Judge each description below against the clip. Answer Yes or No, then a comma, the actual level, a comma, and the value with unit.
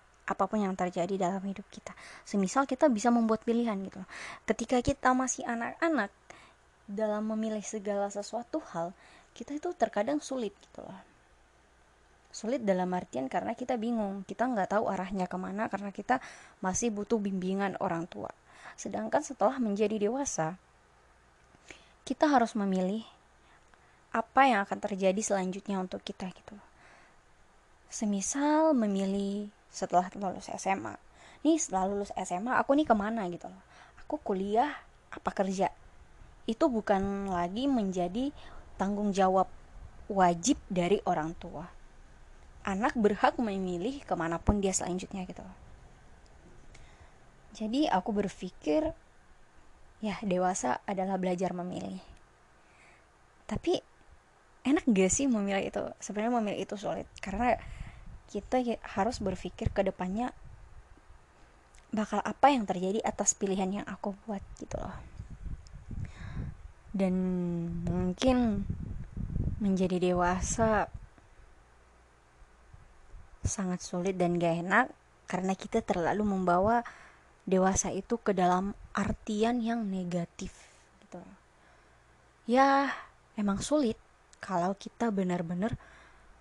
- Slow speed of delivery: No, average, 110 wpm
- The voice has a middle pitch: No, high, 200 Hz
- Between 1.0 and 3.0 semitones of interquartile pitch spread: No, average, 3.9 semitones